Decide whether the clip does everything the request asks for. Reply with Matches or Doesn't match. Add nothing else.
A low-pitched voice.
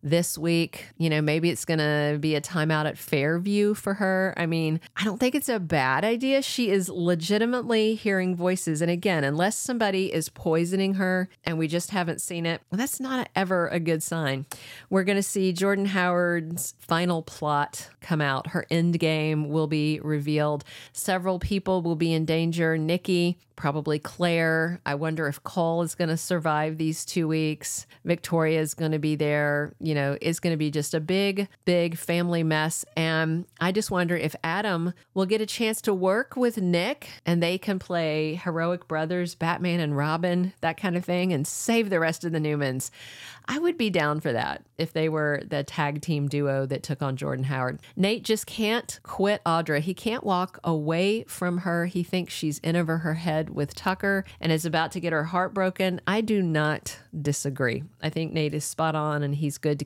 Doesn't match